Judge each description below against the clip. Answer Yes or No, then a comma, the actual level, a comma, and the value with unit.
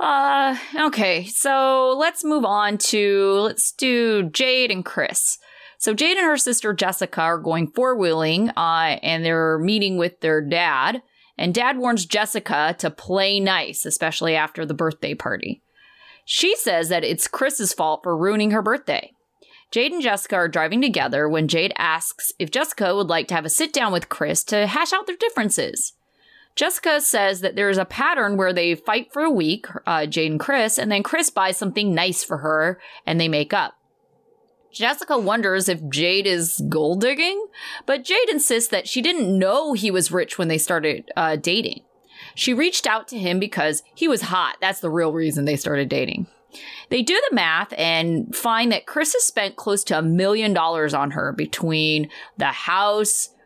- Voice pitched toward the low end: No, high, 195 Hz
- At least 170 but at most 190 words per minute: Yes, average, 185 wpm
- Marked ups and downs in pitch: Yes, wide, 7.2 semitones